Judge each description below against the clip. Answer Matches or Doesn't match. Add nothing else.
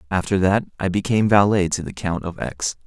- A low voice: Matches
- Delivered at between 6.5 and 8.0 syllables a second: Doesn't match